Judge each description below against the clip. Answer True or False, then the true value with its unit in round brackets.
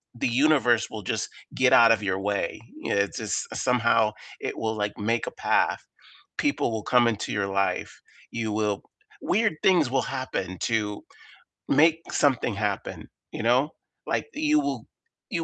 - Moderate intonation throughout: True (4.5 semitones)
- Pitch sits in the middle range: False (115 Hz)